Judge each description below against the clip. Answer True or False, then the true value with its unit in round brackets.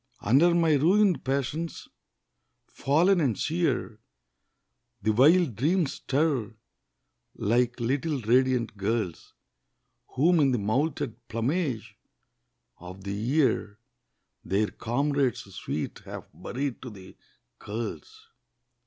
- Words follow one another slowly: True (100 wpm)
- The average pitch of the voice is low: True (130 Hz)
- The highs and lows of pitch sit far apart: True (6.0 semitones)